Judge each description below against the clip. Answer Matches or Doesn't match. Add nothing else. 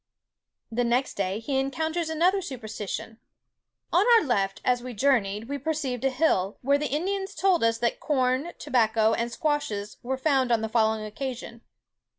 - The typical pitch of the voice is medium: Doesn't match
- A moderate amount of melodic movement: Matches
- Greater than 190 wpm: Doesn't match